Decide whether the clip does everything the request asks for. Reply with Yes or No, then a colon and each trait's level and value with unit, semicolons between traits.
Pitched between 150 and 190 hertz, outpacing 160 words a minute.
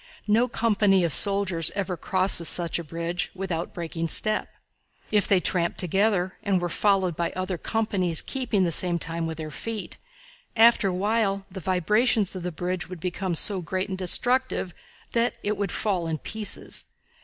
Yes: medium, 185 Hz; average, 170 wpm